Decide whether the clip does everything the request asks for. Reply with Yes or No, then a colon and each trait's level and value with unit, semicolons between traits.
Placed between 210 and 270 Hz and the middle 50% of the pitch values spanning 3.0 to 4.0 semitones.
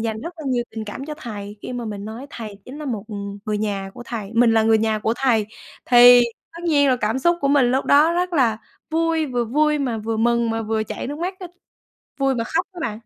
No: high, 240 Hz; average, 4.7 semitones